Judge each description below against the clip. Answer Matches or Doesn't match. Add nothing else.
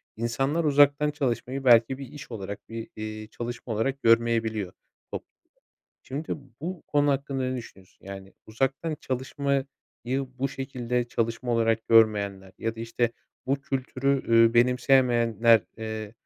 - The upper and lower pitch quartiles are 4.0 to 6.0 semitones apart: Doesn't match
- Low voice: Matches